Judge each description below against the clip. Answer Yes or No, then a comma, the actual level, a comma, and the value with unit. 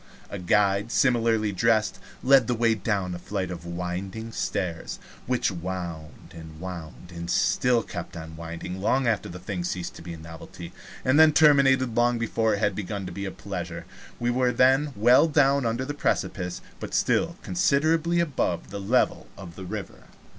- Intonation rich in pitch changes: Yes, wide, 6.1 semitones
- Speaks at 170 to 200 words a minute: Yes, average, 175 wpm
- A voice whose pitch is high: No, low, 100 Hz